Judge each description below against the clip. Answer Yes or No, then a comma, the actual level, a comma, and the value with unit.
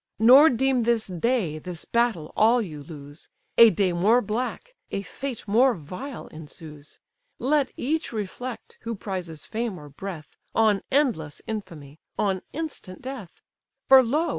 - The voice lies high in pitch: Yes, high, 215 Hz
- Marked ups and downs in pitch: Yes, wide, 6.7 semitones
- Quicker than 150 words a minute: No, average, 140 wpm